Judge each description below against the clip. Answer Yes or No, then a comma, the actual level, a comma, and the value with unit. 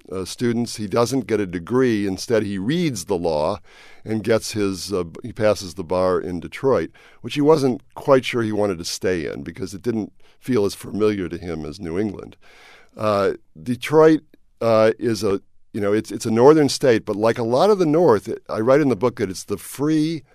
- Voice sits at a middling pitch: No, low, 110 Hz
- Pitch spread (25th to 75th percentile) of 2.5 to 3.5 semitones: No, average, 4.2 semitones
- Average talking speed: No, fast, 210 wpm